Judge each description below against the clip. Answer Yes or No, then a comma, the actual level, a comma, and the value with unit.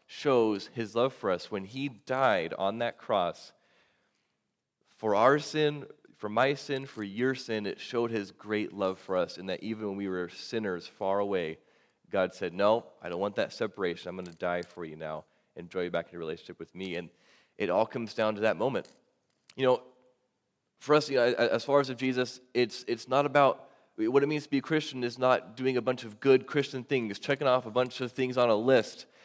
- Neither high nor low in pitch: No, low, 125 Hz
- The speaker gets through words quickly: Yes, fast, 220 wpm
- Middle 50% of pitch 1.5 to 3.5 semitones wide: No, average, 4.4 semitones